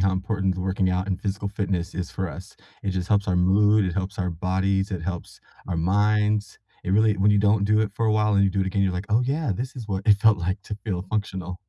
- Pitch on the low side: Yes, low, 100 Hz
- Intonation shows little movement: Yes, narrow, 2.1 semitones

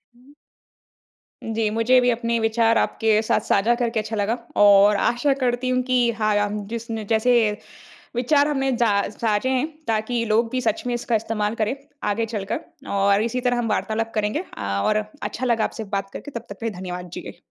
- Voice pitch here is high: Yes, high, 225 Hz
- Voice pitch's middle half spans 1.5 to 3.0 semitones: Yes, narrow, 2.4 semitones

